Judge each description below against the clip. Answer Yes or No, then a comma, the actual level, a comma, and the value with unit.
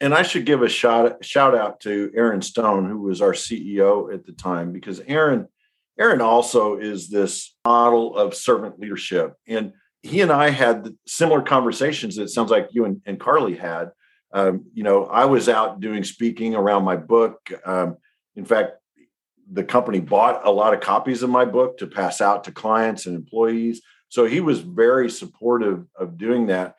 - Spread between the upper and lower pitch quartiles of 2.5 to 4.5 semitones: Yes, average, 3.2 semitones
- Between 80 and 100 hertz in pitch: No, low, 115 Hz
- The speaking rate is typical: Yes, average, 185 wpm